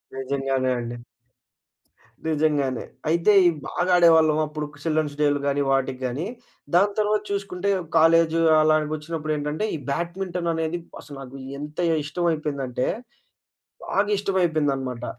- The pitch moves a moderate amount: Yes, average, 3.5 semitones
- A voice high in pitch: No, medium, 155 Hz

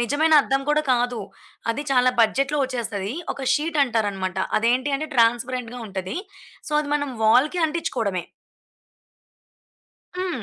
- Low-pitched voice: No, very high, 250 Hz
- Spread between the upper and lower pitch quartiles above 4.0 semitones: Yes, average, 4.4 semitones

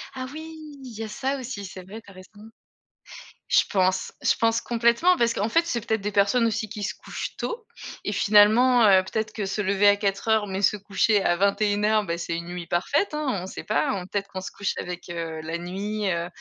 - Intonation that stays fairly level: No, average, 3.2 semitones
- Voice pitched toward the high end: Yes, high, 205 Hz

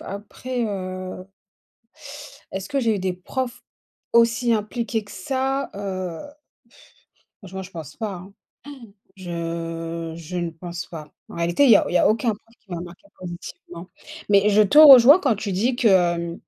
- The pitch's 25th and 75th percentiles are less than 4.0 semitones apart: No, average, 5.1 semitones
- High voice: Yes, high, 195 Hz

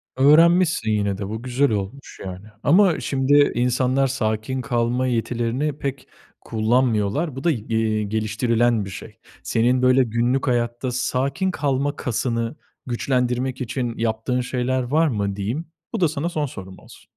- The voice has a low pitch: Yes, low, 125 Hz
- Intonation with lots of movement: No, average, 3.4 semitones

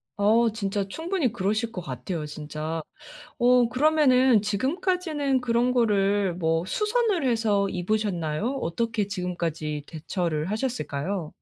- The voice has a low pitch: No, high, 210 Hz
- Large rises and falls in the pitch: Yes, wide, 6.2 semitones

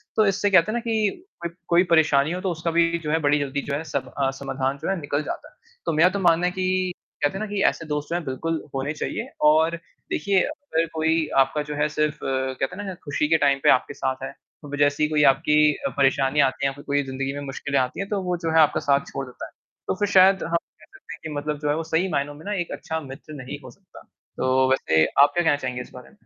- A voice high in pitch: No, medium, 150 Hz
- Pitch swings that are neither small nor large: Yes, average, 4.1 semitones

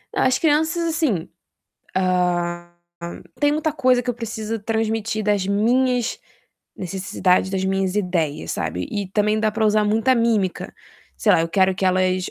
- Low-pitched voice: No, high, 210 Hz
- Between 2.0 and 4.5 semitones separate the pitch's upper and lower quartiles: Yes, average, 4.0 semitones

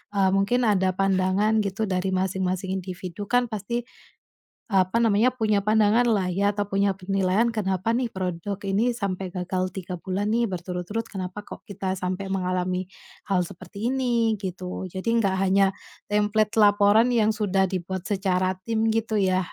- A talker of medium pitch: No, high, 195 Hz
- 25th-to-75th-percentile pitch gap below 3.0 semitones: Yes, narrow, 2.5 semitones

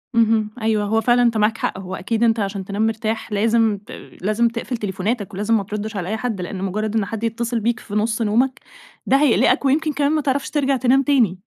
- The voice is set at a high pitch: Yes, high, 225 Hz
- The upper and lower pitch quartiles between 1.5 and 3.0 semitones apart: Yes, narrow, 2.6 semitones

